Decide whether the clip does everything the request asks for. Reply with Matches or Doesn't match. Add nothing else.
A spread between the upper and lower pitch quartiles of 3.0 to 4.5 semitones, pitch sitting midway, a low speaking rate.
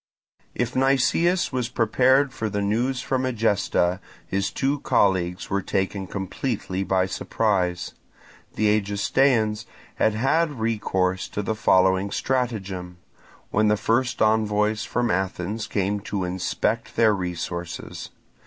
Doesn't match